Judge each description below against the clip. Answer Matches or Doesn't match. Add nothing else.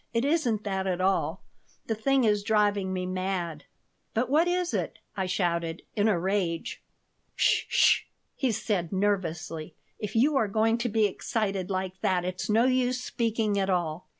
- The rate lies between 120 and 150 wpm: Doesn't match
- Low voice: Doesn't match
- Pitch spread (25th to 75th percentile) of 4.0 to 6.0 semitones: Doesn't match